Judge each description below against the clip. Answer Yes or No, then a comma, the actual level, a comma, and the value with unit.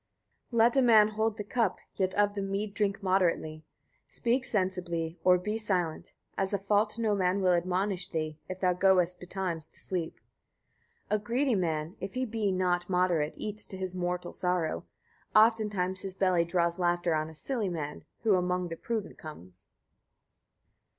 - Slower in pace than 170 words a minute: No, average, 175 wpm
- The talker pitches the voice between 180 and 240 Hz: Yes, medium, 185 Hz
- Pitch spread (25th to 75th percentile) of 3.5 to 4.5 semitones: No, average, 3.0 semitones